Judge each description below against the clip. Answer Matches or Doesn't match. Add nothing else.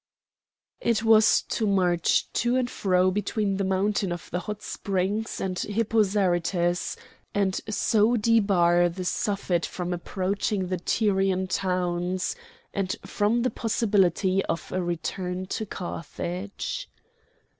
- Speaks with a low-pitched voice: Doesn't match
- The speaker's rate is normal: Doesn't match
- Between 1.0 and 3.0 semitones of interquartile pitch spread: Matches